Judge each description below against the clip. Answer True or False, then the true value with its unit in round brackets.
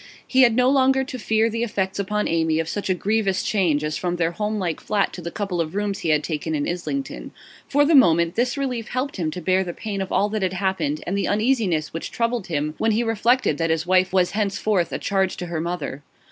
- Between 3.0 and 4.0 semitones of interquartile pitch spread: False (4.8 semitones)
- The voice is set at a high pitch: True (195 Hz)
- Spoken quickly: True (240 wpm)